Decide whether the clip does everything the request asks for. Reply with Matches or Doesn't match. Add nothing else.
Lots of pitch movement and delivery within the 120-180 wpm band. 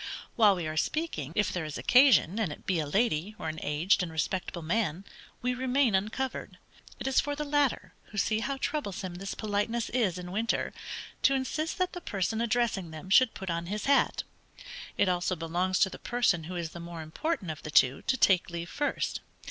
Doesn't match